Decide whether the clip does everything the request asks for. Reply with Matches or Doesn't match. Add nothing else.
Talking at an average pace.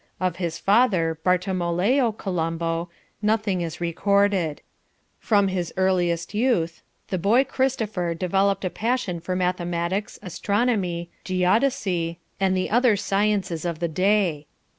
Doesn't match